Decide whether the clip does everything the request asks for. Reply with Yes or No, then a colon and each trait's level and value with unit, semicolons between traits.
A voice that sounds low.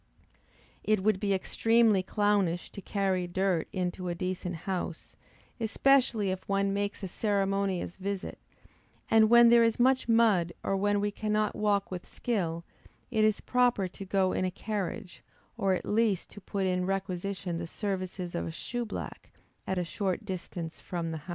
No: high, 195 Hz